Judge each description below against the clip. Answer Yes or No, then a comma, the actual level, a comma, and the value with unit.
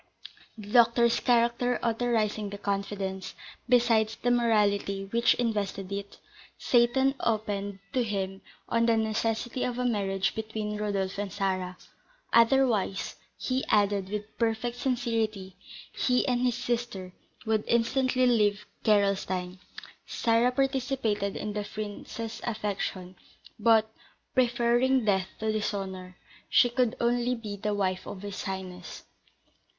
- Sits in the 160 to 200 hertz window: No, high, 220 Hz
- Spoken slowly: Yes, slow, 120 wpm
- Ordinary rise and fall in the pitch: Yes, average, 3.1 semitones